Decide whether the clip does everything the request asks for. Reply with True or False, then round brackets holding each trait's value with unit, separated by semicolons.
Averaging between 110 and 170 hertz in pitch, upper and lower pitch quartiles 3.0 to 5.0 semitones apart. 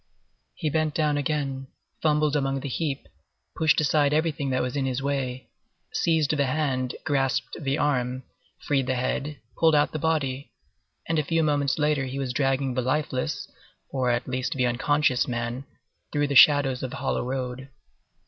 False (140 Hz; 2.5 semitones)